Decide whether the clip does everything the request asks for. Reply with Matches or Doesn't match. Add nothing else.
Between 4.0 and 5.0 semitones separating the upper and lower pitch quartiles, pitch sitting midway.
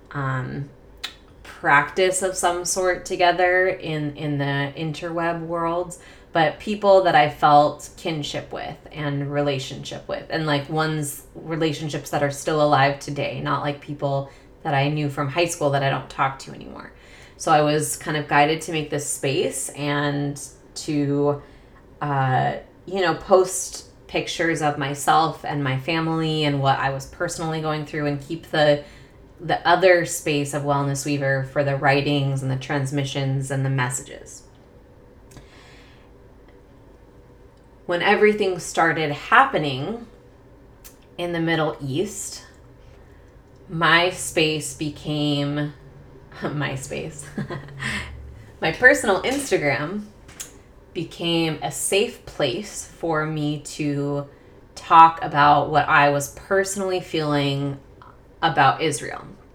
Doesn't match